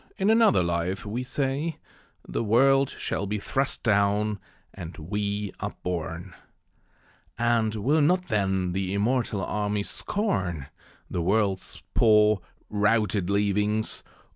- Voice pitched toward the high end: No, low, 105 Hz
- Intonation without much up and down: No, average, 3.7 semitones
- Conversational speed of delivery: No, slow, 115 wpm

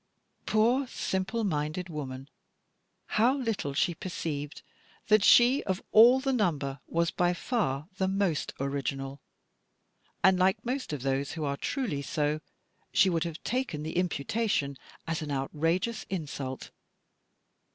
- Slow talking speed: Yes, slow, 130 wpm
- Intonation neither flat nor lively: No, wide, 6.9 semitones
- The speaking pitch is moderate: Yes, medium, 170 Hz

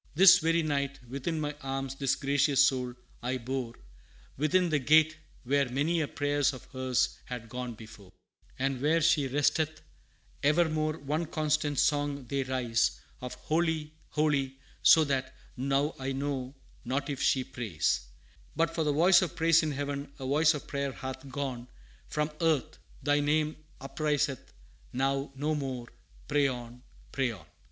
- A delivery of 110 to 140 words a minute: No, average, 155 wpm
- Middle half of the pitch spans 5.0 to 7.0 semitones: No, average, 2.8 semitones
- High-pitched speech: No, medium, 140 Hz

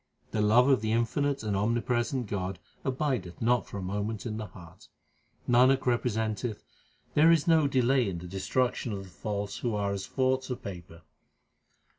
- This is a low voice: Yes, low, 115 Hz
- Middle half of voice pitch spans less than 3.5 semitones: No, average, 4.3 semitones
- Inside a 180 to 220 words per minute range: No, average, 170 wpm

